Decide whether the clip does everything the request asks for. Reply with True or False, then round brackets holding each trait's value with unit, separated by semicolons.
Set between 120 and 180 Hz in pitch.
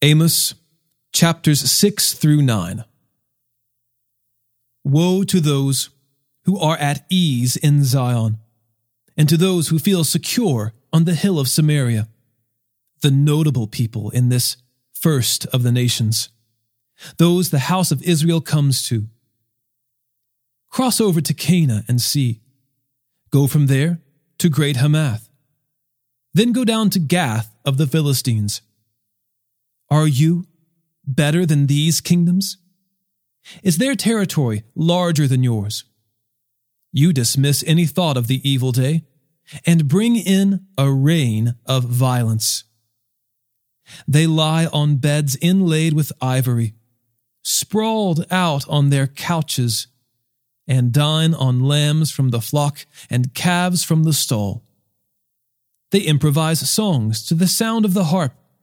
True (140 Hz)